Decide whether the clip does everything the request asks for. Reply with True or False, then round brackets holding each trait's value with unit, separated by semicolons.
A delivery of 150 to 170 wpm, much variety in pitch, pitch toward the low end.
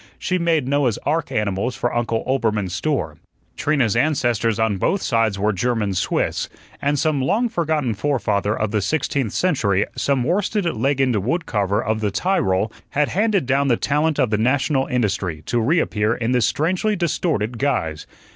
True (165 wpm; 5.9 semitones; 125 Hz)